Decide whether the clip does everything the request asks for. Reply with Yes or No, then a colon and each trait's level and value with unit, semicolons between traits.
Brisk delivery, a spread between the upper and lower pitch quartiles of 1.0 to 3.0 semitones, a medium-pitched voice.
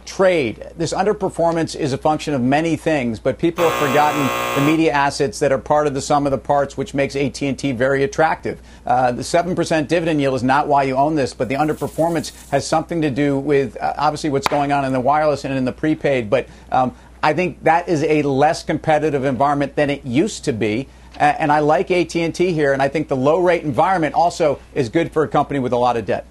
Yes: fast, 230 wpm; narrow, 2.6 semitones; medium, 145 Hz